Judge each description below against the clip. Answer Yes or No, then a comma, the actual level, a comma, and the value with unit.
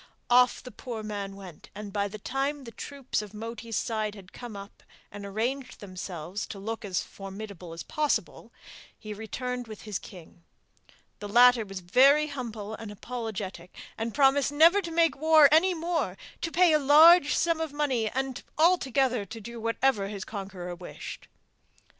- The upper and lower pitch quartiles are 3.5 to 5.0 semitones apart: No, wide, 5.6 semitones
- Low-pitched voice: No, high, 230 Hz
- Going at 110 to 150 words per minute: No, average, 165 wpm